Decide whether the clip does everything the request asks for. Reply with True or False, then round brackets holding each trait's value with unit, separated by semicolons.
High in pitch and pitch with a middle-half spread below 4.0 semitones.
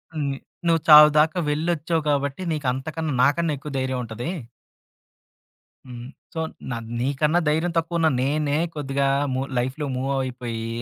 False (145 Hz; 3.3 semitones)